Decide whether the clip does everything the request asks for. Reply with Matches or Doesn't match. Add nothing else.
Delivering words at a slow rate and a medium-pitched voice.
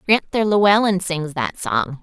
Doesn't match